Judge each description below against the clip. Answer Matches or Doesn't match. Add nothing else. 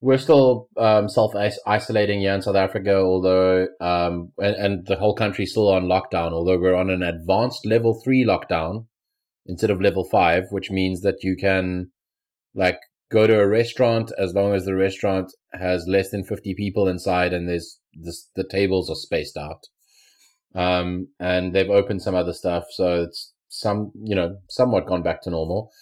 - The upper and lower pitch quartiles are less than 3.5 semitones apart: Matches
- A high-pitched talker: Doesn't match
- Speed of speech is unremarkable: Matches